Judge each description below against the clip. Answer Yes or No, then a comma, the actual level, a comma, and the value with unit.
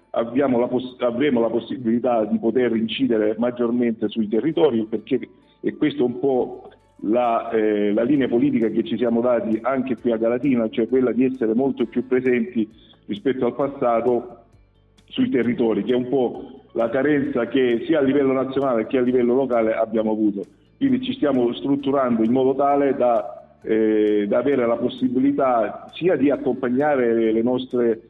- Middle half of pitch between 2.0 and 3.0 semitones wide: Yes, narrow, 2.5 semitones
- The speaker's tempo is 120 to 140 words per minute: No, average, 165 wpm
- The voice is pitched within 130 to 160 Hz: No, low, 120 Hz